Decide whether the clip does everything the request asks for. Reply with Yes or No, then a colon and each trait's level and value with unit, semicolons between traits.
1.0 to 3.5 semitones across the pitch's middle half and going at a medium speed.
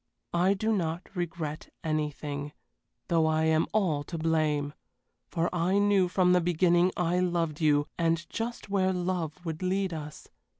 Yes: average, 2.7 semitones; average, 155 wpm